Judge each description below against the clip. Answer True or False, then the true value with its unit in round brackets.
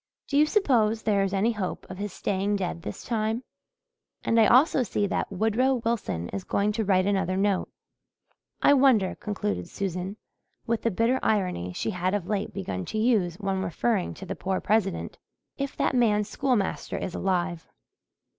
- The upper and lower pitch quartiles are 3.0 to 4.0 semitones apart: True (3.3 semitones)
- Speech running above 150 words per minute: True (175 wpm)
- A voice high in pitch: True (205 Hz)